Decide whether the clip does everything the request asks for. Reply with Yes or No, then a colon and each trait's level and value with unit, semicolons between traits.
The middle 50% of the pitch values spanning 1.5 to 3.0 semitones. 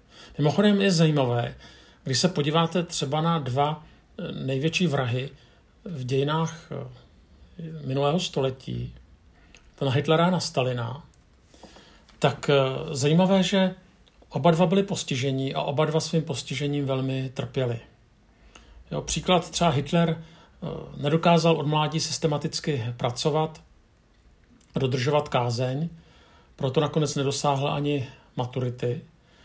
No: average, 3.7 semitones